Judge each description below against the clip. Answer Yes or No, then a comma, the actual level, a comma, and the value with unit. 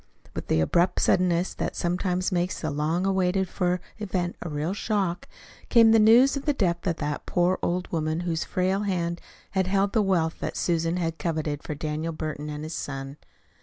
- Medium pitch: Yes, medium, 175 Hz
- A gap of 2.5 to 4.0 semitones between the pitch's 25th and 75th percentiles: Yes, average, 2.9 semitones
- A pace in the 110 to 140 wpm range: No, average, 190 wpm